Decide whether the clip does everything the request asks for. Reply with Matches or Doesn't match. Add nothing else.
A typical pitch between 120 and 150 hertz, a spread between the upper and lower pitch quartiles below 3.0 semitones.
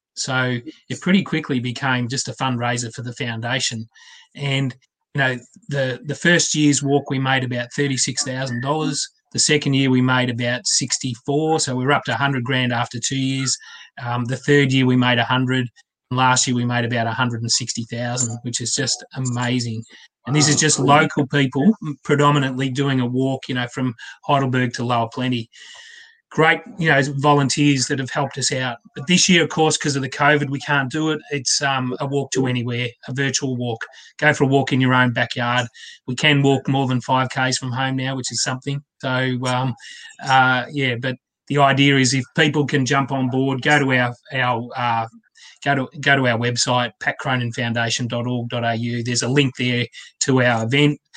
Matches